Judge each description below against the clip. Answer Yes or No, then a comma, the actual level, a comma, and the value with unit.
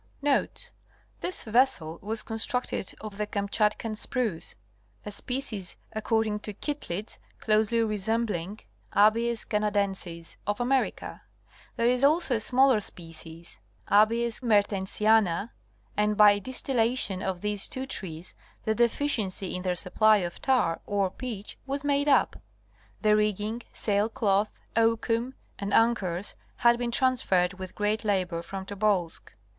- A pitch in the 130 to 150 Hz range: No, high, 215 Hz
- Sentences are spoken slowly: Yes, slow, 120 wpm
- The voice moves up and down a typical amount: Yes, average, 3.3 semitones